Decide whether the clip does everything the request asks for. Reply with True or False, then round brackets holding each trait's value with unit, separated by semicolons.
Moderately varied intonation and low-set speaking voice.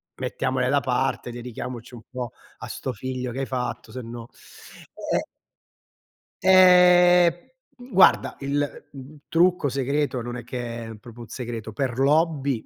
True (3.2 semitones; 130 Hz)